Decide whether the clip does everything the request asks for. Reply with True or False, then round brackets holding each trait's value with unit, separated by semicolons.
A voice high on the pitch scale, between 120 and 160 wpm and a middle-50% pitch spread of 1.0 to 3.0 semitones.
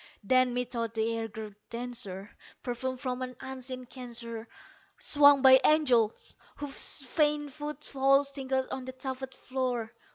True (255 Hz; 135 wpm; 2.4 semitones)